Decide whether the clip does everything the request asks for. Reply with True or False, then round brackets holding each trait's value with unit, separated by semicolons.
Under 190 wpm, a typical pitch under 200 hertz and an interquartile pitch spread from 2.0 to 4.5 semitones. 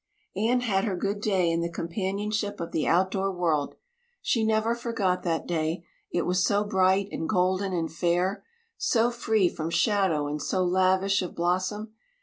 True (165 wpm; 190 Hz; 3.1 semitones)